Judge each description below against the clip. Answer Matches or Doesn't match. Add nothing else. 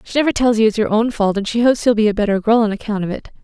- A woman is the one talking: Matches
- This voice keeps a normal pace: Doesn't match